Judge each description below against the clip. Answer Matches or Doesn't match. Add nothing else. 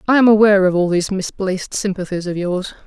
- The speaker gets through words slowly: Doesn't match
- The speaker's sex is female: Matches